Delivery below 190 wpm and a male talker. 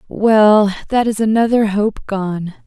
No: slow, 135 wpm; female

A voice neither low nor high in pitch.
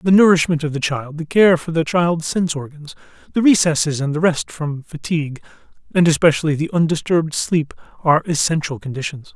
Yes: medium, 160 Hz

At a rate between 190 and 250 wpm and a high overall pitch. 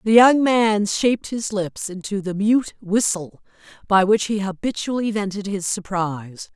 No: average, 155 wpm; high, 205 Hz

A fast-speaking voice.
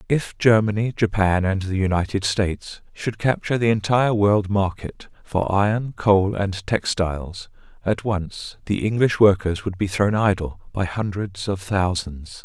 No: average, 150 wpm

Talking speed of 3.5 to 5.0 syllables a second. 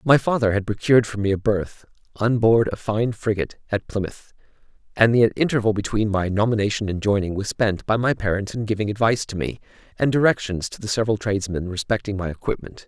No: 6.1 syllables/s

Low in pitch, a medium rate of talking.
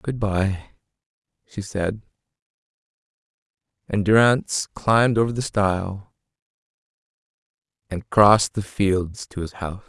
No: low, 100 Hz; slow, 105 wpm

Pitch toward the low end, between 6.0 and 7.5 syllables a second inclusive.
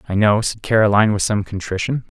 Yes: low, 105 Hz; 6.3 syllables/s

